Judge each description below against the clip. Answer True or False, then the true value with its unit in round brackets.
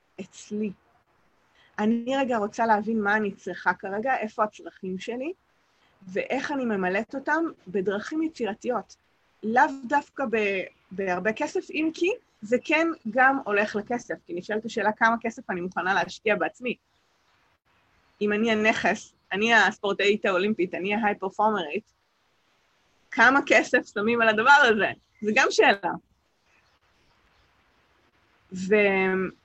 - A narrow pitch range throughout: False (4.2 semitones)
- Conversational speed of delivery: False (115 wpm)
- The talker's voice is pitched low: False (215 Hz)